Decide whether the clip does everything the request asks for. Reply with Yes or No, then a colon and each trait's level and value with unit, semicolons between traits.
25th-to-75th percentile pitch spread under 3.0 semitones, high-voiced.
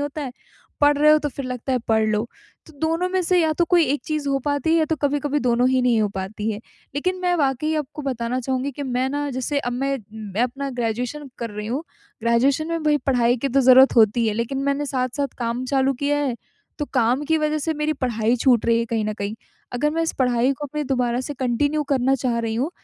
No: average, 3.4 semitones; very high, 265 Hz